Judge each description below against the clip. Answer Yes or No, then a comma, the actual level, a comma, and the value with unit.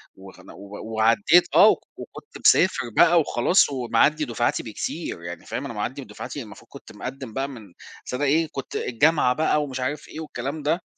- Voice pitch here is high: No, low, 135 Hz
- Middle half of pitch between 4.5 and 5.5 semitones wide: Yes, average, 4.9 semitones